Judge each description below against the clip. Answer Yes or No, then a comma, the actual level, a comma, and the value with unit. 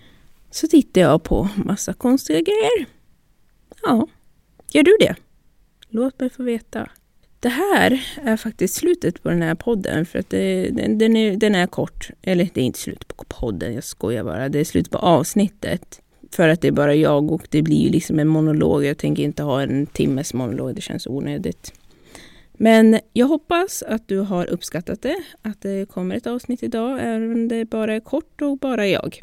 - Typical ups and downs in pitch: No, wide, 7.0 semitones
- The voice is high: Yes, high, 220 Hz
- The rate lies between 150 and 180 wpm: No, fast, 195 wpm